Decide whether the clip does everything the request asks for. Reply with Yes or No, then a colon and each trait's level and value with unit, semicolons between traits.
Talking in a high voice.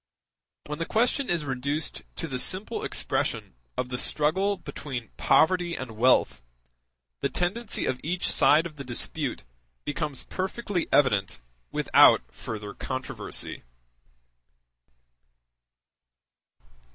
No: medium, 150 Hz